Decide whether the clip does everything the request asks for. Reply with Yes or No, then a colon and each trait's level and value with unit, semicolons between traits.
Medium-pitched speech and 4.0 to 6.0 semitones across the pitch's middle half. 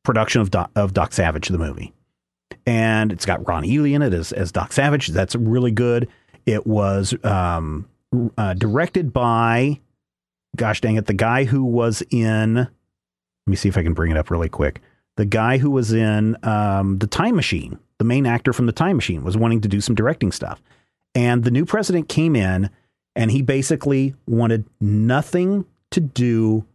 No: low, 110 Hz; average, 4.5 semitones